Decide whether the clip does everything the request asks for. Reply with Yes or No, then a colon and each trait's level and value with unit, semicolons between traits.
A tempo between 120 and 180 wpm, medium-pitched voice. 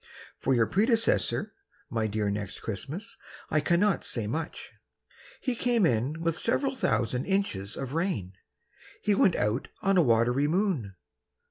Yes: average, 140 wpm; medium, 155 Hz